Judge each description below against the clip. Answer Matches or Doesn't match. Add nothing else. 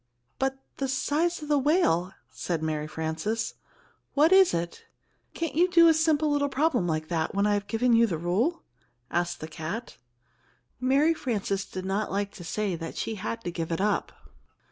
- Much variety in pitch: Matches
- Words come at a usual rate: Matches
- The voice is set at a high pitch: Matches